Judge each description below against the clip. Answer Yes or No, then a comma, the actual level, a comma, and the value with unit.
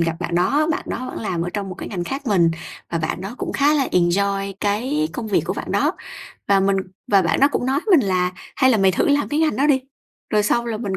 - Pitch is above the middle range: Yes, high, 205 Hz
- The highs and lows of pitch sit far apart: Yes, wide, 6.5 semitones